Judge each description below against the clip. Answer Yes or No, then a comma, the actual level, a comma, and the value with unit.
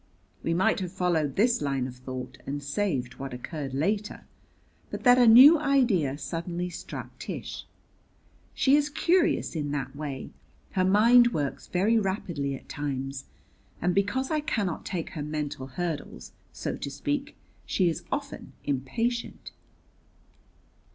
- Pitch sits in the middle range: Yes, medium, 170 Hz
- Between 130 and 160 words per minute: Yes, average, 140 wpm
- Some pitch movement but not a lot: No, wide, 8.5 semitones